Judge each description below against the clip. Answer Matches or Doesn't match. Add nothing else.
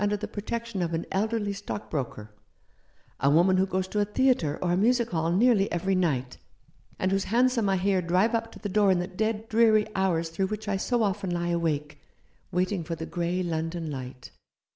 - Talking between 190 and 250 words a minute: Matches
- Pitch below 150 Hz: Doesn't match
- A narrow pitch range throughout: Doesn't match